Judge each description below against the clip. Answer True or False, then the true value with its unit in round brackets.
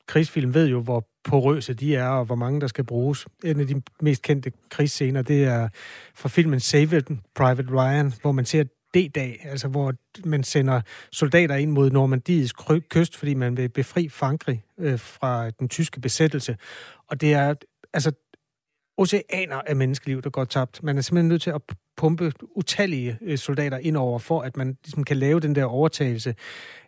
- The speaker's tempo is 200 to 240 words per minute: False (180 wpm)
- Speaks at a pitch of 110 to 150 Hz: True (140 Hz)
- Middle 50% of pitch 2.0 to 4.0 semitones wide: True (3.0 semitones)